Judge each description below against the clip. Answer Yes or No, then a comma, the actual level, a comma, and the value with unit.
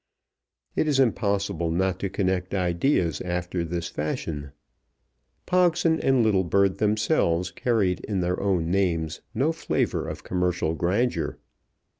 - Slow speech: Yes, slow, 120 wpm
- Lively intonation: No, average, 4.0 semitones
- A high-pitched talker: No, very low, 95 Hz